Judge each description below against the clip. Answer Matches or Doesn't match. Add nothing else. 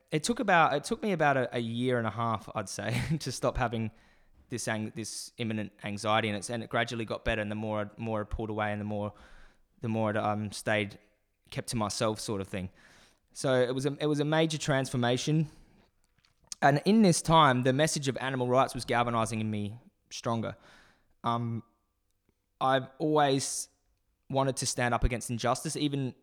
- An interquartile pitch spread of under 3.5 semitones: Doesn't match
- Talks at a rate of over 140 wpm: Matches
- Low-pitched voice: Matches